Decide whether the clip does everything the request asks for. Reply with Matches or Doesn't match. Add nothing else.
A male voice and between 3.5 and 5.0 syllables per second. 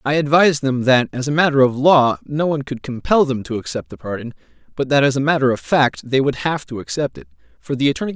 Doesn't match